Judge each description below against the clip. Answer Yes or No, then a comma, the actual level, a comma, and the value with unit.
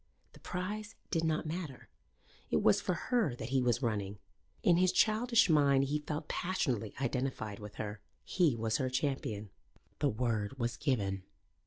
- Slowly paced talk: No, average, 160 wpm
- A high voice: No, low, 135 Hz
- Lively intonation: Yes, wide, 6.8 semitones